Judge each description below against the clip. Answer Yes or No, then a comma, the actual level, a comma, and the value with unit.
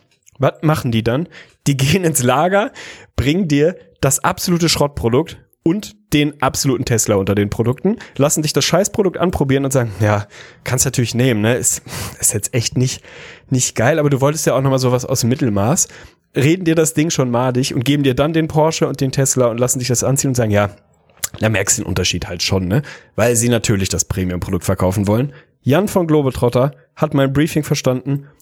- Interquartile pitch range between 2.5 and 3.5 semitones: No, average, 4.3 semitones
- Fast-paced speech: Yes, fast, 200 wpm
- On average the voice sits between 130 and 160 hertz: Yes, low, 135 Hz